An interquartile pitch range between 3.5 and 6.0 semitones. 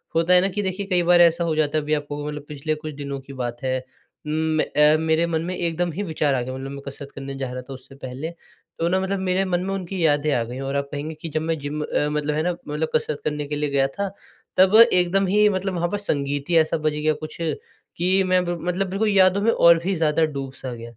Yes: average, 4.0 semitones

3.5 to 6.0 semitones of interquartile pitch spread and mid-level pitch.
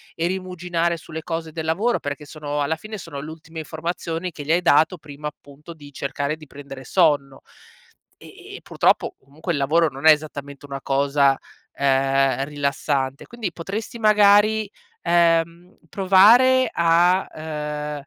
Yes: average, 3.8 semitones; medium, 160 Hz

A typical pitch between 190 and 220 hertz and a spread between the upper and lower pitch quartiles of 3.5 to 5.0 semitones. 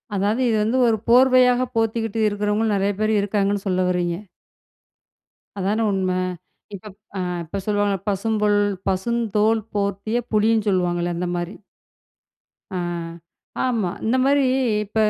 No: high, 210 Hz; average, 2.7 semitones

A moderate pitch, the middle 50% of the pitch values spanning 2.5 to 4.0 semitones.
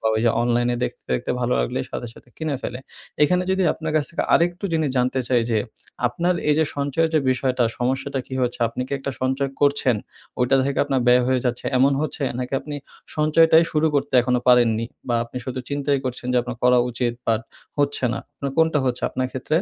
No: low, 130 Hz; average, 3.1 semitones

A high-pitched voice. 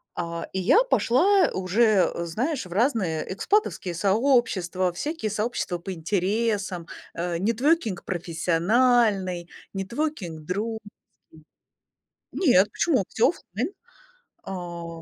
Yes: high, 195 Hz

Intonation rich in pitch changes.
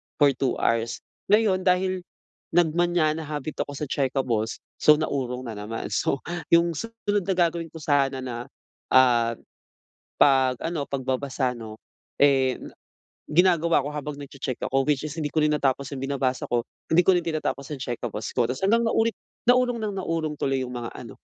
No: average, 4.7 semitones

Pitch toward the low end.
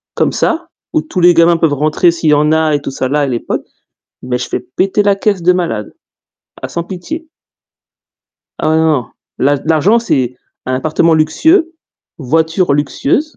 No: medium, 160 Hz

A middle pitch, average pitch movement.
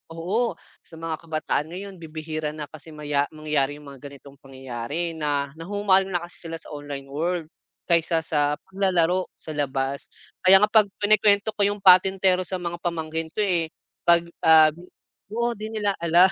Yes: medium, 165 Hz; average, 4.2 semitones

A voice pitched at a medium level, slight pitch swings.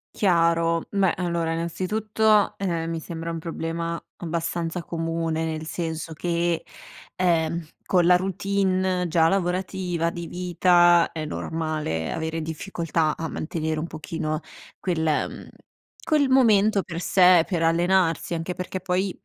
Yes: medium, 170 Hz; narrow, 2.0 semitones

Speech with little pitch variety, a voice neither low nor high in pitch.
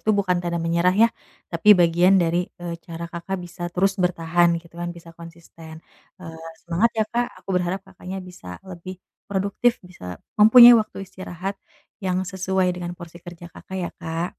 Yes: narrow, 2.0 semitones; medium, 180 Hz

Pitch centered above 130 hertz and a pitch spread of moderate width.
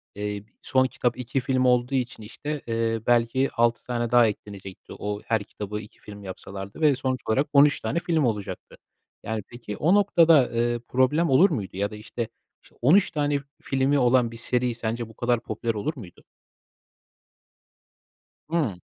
No: low, 120 Hz; average, 3.7 semitones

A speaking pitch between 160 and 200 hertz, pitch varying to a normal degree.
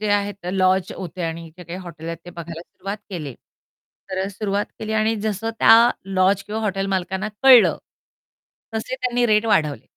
Yes: high, 195 Hz; average, 3.5 semitones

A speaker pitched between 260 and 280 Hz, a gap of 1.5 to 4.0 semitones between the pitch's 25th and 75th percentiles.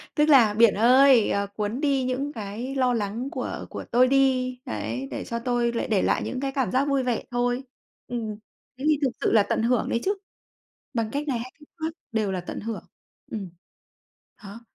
No: high, 245 Hz; average, 3.6 semitones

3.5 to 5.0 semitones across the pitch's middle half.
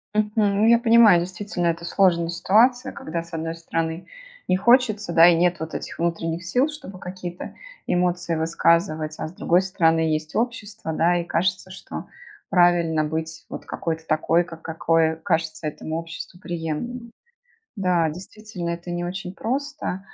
No: average, 3.0 semitones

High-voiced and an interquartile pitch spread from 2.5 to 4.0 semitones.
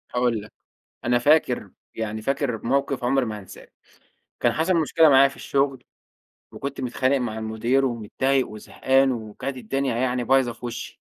No: low, 130 Hz; average, 3.0 semitones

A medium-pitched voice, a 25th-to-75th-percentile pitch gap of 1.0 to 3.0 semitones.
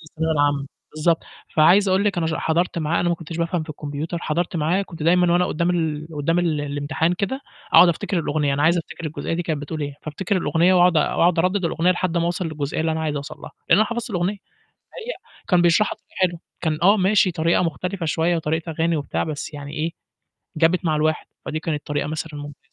Yes: medium, 165 Hz; narrow, 2.5 semitones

